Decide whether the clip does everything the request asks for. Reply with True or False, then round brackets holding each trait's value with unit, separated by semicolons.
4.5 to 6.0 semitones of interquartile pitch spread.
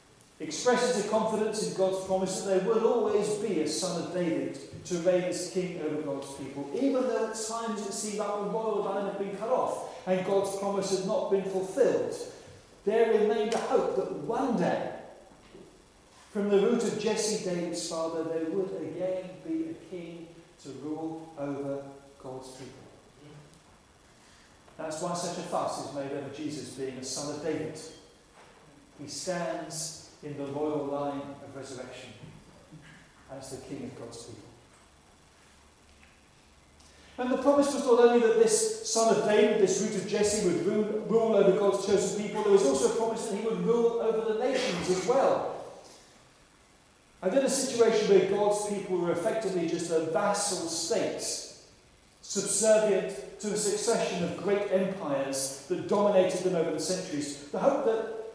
True (5.4 semitones)